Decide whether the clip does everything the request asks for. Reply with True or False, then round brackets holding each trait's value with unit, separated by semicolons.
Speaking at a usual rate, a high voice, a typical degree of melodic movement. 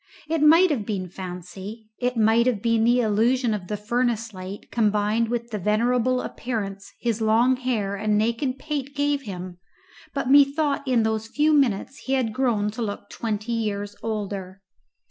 True (165 wpm; 225 Hz; 3.5 semitones)